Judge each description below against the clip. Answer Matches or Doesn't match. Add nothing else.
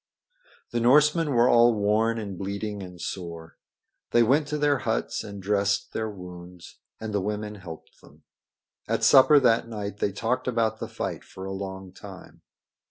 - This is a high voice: Doesn't match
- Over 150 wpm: Matches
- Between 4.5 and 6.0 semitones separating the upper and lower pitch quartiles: Doesn't match